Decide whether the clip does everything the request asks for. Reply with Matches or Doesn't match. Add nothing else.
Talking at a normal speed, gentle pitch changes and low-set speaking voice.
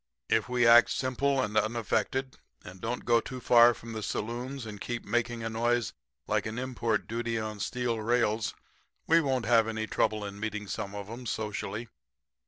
Matches